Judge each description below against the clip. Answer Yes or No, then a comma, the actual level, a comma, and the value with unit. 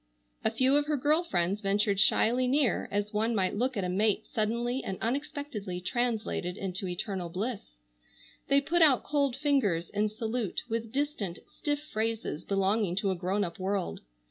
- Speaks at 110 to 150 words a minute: No, average, 170 wpm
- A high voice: Yes, high, 215 Hz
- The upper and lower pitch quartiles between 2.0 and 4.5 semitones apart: No, average, 4.9 semitones